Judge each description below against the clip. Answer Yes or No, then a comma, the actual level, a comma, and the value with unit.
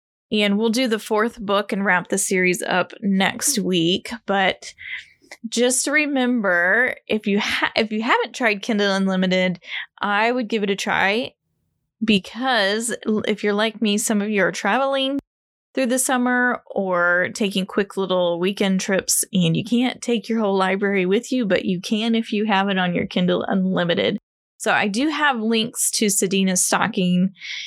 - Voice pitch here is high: Yes, high, 210 Hz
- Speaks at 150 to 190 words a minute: Yes, average, 170 wpm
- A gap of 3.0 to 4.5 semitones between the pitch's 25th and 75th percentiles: Yes, average, 3.6 semitones